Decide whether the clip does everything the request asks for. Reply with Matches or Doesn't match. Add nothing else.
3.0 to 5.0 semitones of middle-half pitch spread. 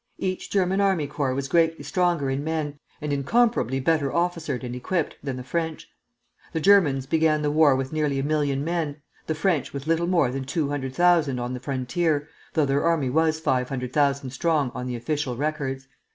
Matches